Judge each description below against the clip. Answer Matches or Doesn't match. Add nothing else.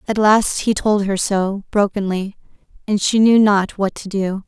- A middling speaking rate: Matches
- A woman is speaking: Matches